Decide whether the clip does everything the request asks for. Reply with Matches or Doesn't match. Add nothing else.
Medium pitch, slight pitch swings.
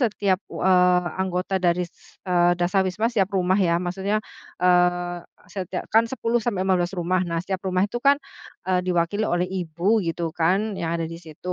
Matches